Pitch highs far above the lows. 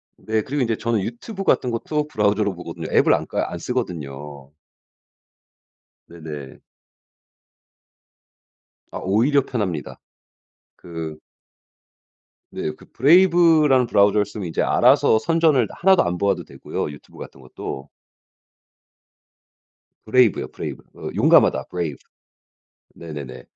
Yes: wide, 8.0 semitones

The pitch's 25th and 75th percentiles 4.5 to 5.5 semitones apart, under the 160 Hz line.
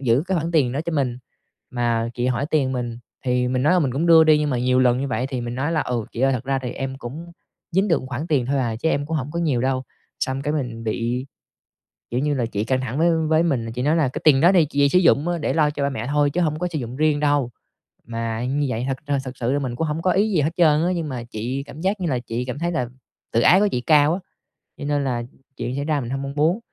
No: average, 3.8 semitones; medium, 140 Hz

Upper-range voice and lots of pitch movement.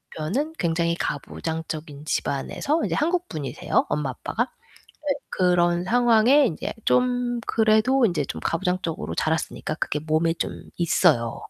No: medium, 175 Hz; wide, 7.6 semitones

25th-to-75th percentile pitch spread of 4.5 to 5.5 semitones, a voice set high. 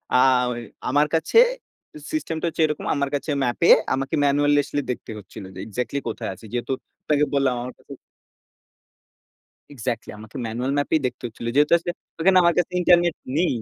No: average, 4.8 semitones; medium, 145 Hz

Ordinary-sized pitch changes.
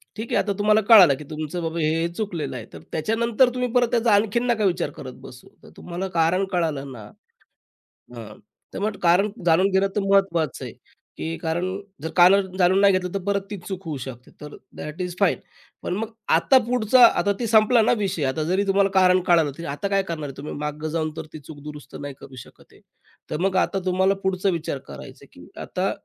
Yes: average, 4.4 semitones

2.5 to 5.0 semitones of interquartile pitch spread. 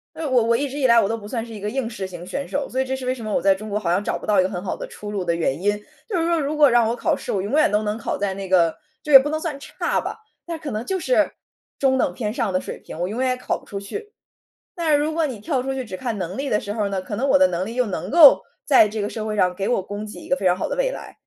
No: wide, 5.6 semitones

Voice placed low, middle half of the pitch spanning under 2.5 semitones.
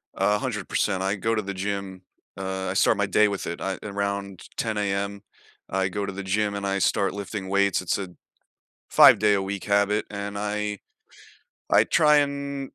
Yes: low, 100 Hz; narrow, 1.4 semitones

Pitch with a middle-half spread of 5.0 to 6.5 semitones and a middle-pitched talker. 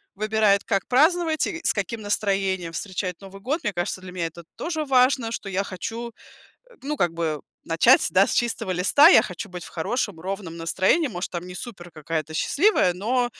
No: wide, 5.4 semitones; high, 195 Hz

